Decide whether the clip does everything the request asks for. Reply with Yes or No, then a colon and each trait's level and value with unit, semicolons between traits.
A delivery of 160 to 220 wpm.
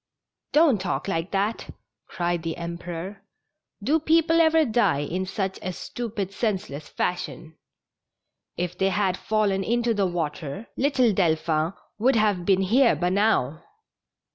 No: average, 150 wpm